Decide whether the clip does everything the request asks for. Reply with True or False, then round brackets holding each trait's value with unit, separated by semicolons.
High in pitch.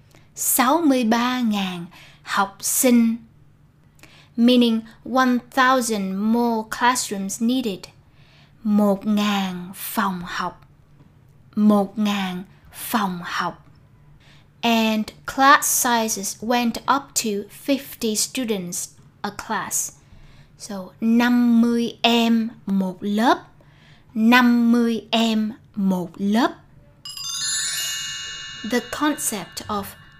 True (210 Hz)